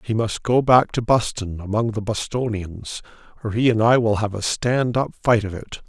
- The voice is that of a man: Yes, male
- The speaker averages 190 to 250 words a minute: Yes, fast, 205 wpm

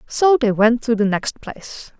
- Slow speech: No, fast, 210 wpm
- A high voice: Yes, high, 235 Hz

